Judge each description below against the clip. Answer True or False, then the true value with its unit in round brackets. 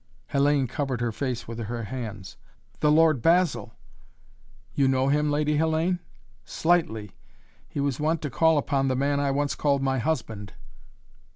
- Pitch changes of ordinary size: True (3.9 semitones)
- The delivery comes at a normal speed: True (155 wpm)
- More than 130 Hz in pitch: True (140 Hz)